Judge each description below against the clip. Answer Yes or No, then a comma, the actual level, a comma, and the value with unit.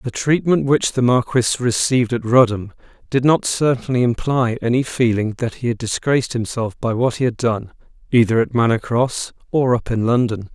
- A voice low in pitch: Yes, low, 120 Hz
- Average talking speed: Yes, average, 180 wpm